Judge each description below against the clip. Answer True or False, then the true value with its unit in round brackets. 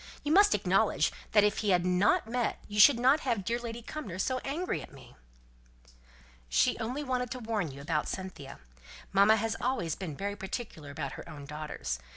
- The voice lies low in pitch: False (210 Hz)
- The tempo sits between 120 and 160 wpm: False (195 wpm)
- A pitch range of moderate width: False (6.8 semitones)